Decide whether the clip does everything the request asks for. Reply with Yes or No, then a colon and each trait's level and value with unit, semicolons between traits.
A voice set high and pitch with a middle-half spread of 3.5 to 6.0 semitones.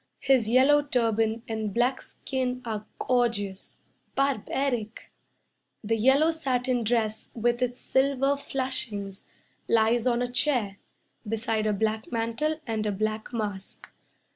No: high, 235 Hz; average, 3.1 semitones